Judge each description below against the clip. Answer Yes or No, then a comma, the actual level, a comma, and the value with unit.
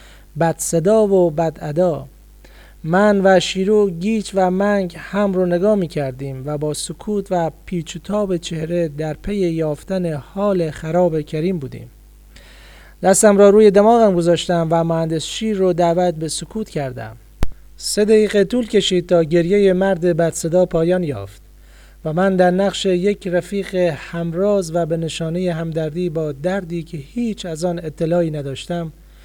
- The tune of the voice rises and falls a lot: No, average, 3.3 semitones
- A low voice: No, medium, 175 Hz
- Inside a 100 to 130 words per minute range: No, average, 150 wpm